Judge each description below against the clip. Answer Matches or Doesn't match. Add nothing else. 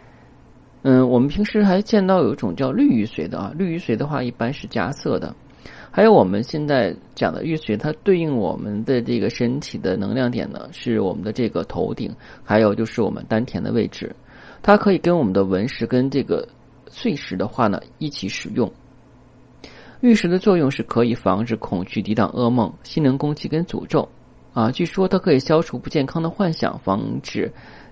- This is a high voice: Doesn't match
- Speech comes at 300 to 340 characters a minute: Doesn't match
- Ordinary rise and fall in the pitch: Doesn't match